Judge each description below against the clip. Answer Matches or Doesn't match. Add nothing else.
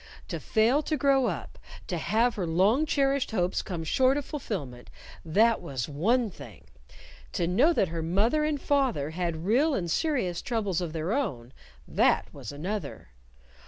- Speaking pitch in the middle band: Doesn't match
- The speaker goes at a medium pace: Matches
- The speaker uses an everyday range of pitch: Doesn't match